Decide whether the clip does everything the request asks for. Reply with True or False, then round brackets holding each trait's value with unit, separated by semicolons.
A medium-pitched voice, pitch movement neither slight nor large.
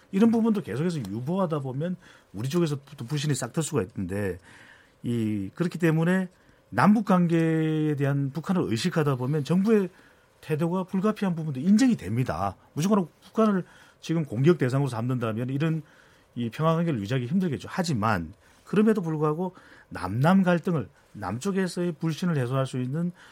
False (155 Hz; 5.8 semitones)